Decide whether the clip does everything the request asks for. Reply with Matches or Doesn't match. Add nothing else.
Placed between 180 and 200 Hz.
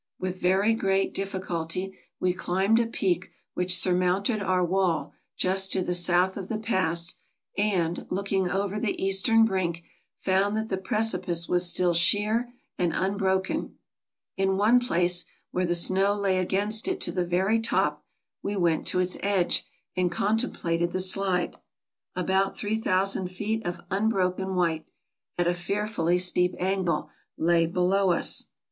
Matches